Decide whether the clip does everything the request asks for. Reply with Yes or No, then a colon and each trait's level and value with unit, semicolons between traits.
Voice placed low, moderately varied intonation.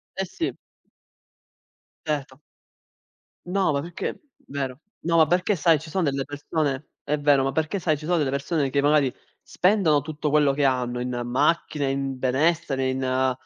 No: medium, 145 Hz; average, 3.2 semitones